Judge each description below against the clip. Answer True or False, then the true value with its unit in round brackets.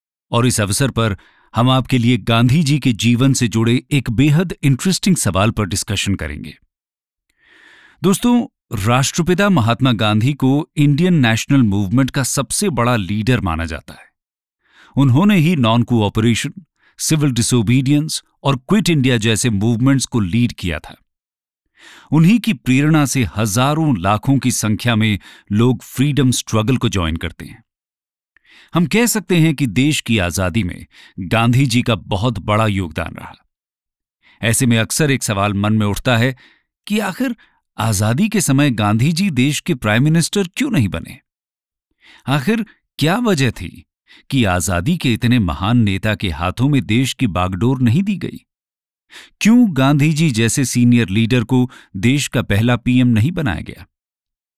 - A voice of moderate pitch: False (125 Hz)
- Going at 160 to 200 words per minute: False (150 wpm)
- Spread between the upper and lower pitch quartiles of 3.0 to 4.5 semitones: False (4.9 semitones)